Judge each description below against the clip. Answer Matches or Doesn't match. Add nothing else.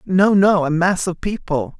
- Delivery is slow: Doesn't match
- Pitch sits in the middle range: Matches